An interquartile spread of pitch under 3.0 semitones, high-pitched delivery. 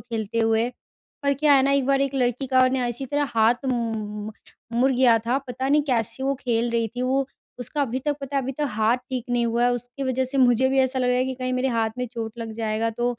Yes: narrow, 2.4 semitones; very high, 250 Hz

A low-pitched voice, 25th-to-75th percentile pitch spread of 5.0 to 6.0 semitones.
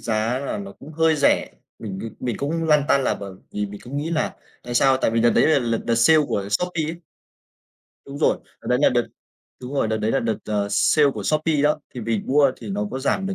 Yes: low, 130 Hz; wide, 5.5 semitones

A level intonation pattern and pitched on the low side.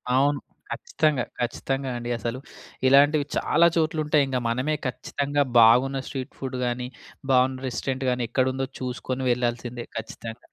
Yes: narrow, 2.3 semitones; low, 130 Hz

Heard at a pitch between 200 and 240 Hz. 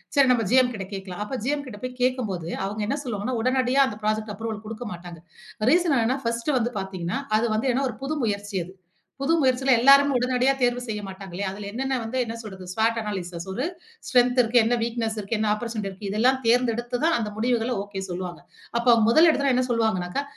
Yes: high, 230 Hz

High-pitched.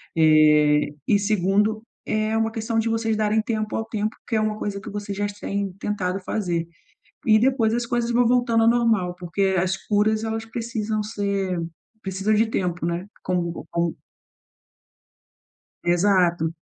Yes: high, 205 Hz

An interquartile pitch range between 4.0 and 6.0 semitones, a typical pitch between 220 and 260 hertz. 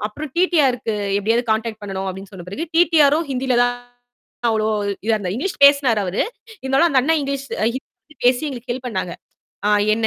Yes: average, 4.6 semitones; very high, 250 Hz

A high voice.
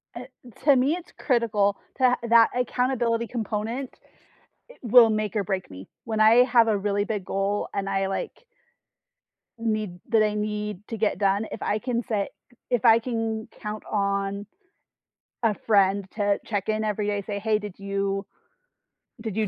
Yes: high, 215 Hz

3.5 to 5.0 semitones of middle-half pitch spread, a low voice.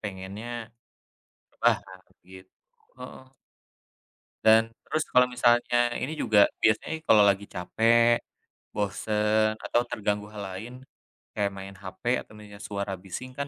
No: average, 2.9 semitones; low, 105 Hz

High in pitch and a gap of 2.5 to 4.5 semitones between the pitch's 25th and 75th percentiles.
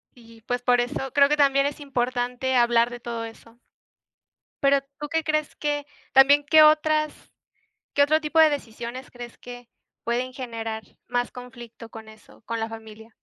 Yes: high, 245 Hz; average, 3.5 semitones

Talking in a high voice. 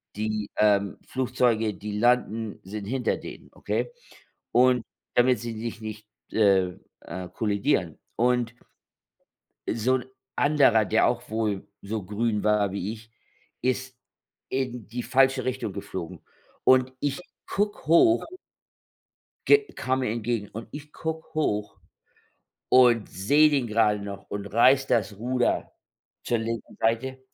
No: low, 115 Hz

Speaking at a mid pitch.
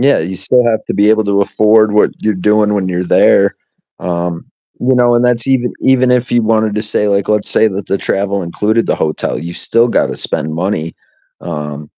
No: low, 105 Hz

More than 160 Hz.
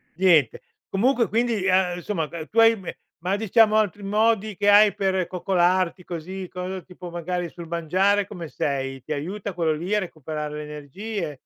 Yes: medium, 185 Hz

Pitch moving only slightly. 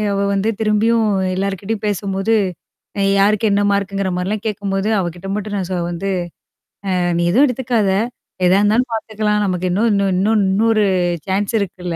Yes: narrow, 1.9 semitones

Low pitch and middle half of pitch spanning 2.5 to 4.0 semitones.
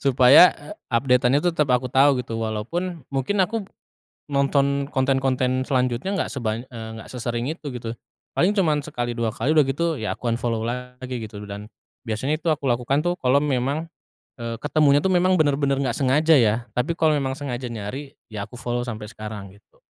Yes: low, 130 Hz; average, 3.6 semitones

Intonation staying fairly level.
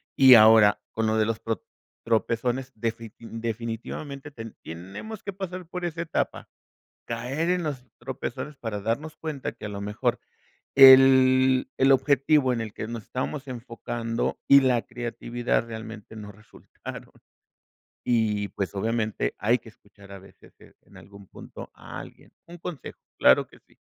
No: average, 3.4 semitones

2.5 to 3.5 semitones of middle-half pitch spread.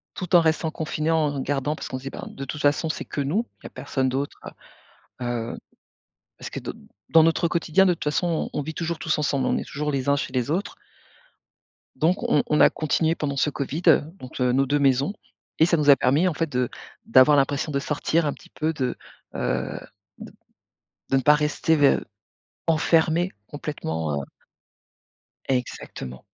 Yes: average, 2.9 semitones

